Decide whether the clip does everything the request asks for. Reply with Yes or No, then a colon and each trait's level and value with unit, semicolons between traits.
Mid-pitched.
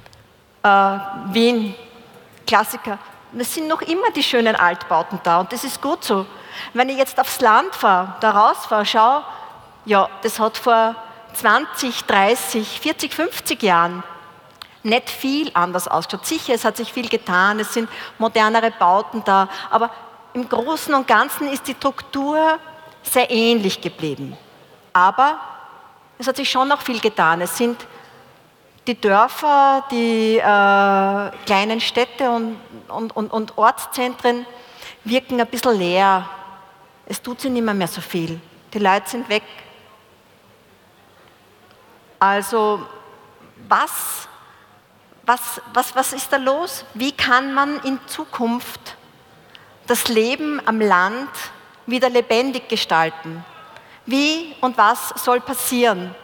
No: high, 230 Hz